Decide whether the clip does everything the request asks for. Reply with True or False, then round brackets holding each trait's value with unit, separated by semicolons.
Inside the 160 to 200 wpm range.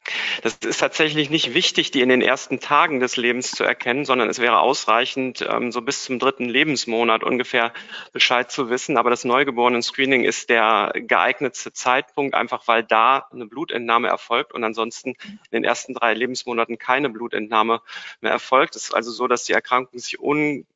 True (175 wpm)